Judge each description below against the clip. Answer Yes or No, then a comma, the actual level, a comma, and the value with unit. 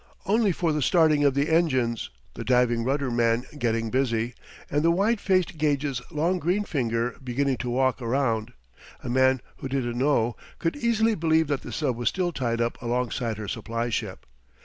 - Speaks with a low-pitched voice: Yes, low, 130 Hz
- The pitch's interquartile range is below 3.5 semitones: No, average, 5.2 semitones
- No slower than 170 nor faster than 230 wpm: Yes, average, 180 wpm